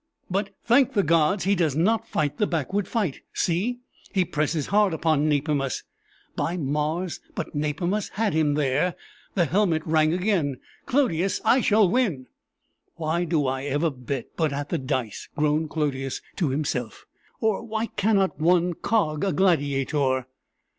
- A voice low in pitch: No, medium, 160 Hz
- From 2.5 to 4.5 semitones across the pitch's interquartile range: No, average, 5.1 semitones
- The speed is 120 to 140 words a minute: No, average, 150 wpm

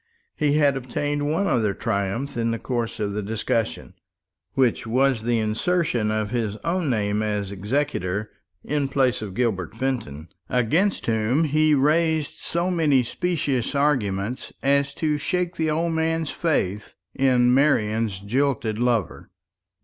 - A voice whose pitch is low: Yes, low, 125 Hz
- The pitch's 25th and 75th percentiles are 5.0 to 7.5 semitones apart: Yes, wide, 5.6 semitones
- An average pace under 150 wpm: Yes, average, 140 wpm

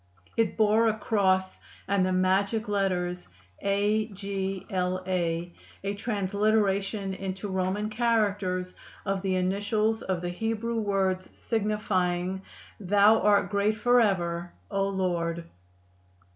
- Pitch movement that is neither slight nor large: No, narrow, 2.3 semitones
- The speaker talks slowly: Yes, slow, 115 wpm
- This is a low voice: No, high, 195 Hz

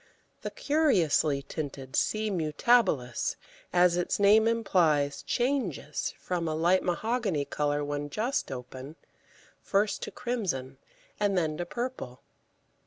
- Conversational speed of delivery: No, slow, 115 wpm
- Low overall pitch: No, medium, 175 Hz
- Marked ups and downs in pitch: Yes, wide, 7.0 semitones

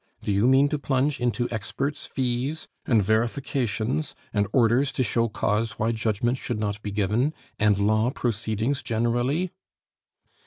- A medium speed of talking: Yes, average, 145 wpm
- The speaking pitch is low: Yes, low, 120 Hz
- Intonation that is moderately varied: Yes, average, 3.6 semitones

